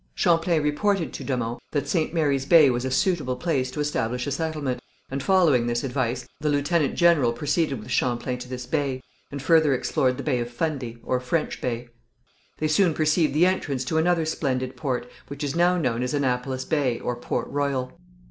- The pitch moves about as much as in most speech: Yes, average, 3.9 semitones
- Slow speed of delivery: No, average, 195 wpm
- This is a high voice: No, medium, 140 Hz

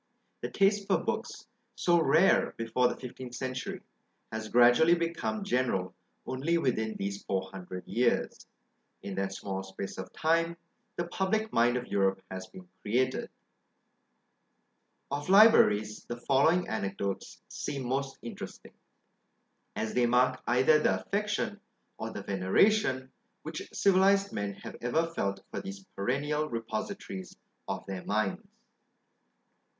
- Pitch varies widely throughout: Yes, wide, 8.6 semitones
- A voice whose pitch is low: Yes, low, 130 Hz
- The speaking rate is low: Yes, slow, 130 wpm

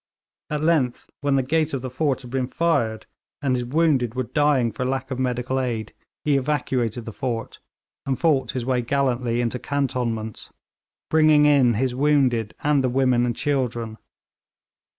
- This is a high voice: No, low, 130 Hz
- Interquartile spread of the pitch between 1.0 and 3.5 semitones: Yes, average, 2.8 semitones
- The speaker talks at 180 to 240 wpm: No, average, 165 wpm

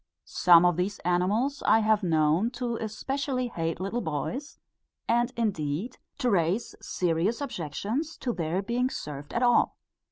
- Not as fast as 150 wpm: Yes, average, 140 wpm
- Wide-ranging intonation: Yes, wide, 6.3 semitones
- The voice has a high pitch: Yes, high, 205 Hz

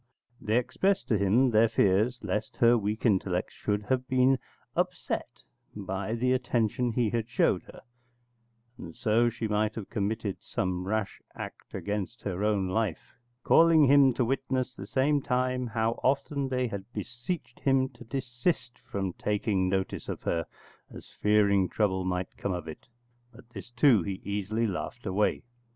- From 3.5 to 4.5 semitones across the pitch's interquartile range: Yes, average, 4.0 semitones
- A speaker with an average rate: Yes, average, 160 wpm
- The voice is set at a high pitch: No, low, 110 Hz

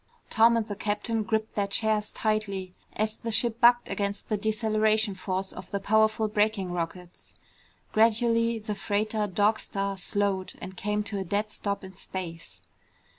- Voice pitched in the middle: No, high, 210 Hz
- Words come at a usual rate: Yes, average, 160 wpm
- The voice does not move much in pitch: Yes, narrow, 1.8 semitones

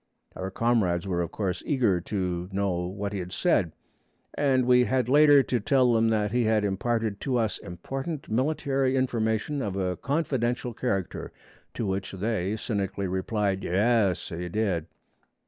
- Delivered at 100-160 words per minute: Yes, average, 155 wpm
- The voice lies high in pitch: No, low, 110 Hz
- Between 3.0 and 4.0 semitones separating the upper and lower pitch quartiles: No, average, 4.6 semitones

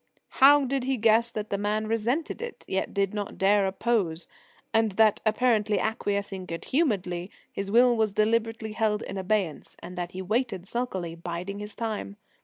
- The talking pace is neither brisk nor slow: Yes, average, 170 wpm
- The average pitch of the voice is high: Yes, high, 210 Hz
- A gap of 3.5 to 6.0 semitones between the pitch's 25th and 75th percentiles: No, average, 3.1 semitones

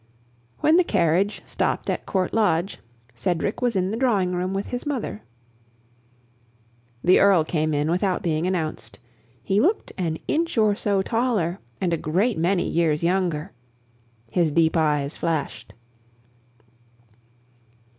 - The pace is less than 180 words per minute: Yes, slow, 135 wpm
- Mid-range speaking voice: Yes, medium, 180 Hz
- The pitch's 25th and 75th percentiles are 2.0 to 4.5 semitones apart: Yes, average, 4.2 semitones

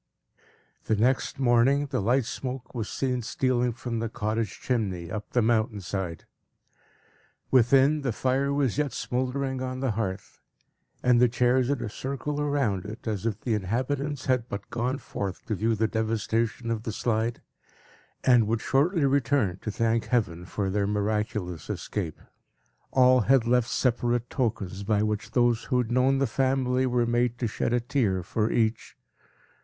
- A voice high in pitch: No, low, 120 Hz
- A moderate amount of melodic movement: Yes, average, 3.2 semitones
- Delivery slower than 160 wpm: No, average, 165 wpm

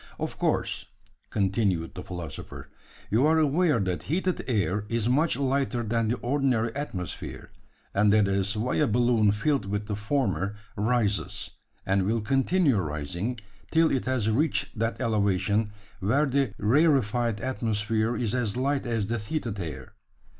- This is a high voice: No, low, 115 Hz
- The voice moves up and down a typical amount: Yes, average, 4.4 semitones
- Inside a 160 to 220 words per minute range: No, average, 145 wpm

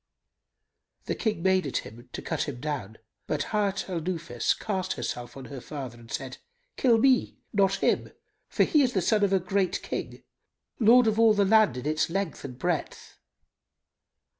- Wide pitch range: Yes, wide, 7.4 semitones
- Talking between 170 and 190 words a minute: Yes, average, 180 wpm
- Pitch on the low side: No, medium, 185 Hz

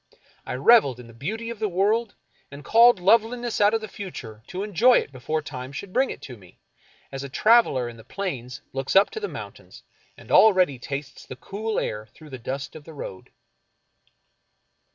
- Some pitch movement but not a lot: No, wide, 8.9 semitones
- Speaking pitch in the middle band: Yes, medium, 170 Hz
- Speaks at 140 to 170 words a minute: No, average, 195 wpm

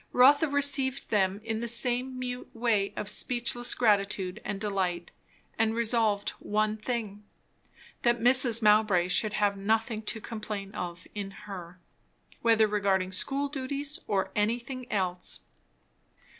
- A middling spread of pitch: Yes, average, 3.4 semitones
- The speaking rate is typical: No, slow, 130 wpm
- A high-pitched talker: Yes, high, 215 Hz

